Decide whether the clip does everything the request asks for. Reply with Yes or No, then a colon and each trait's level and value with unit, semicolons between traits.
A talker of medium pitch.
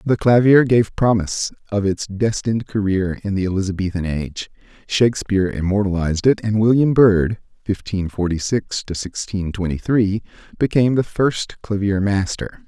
No: low, 100 Hz